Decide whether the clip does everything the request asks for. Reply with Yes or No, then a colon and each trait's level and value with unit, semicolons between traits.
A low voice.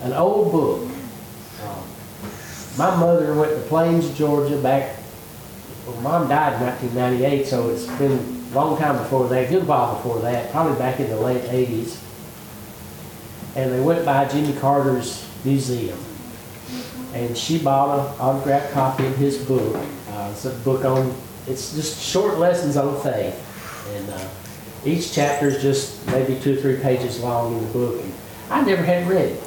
Yes: low, 130 Hz